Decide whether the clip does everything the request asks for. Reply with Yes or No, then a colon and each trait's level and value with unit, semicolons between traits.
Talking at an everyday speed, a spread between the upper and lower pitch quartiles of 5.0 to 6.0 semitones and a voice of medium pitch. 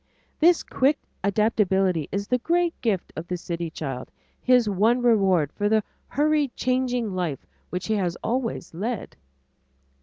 No: average, 145 wpm; wide, 5.6 semitones; high, 210 Hz